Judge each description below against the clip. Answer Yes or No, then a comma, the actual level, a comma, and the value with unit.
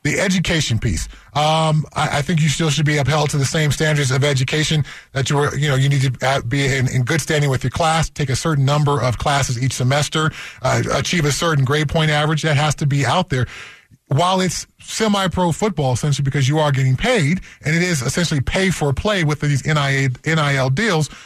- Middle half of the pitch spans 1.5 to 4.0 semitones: Yes, average, 2.8 semitones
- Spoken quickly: Yes, fast, 215 wpm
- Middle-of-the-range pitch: Yes, medium, 145 Hz